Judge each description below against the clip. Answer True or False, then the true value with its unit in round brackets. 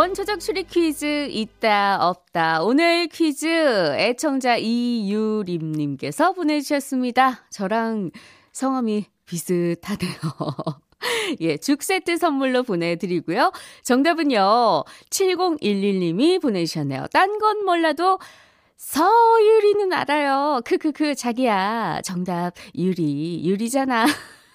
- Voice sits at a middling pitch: False (255 Hz)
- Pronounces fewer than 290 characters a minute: True (225 characters per minute)